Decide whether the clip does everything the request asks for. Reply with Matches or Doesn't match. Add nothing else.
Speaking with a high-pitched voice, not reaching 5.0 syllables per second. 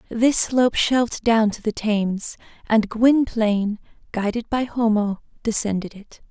Matches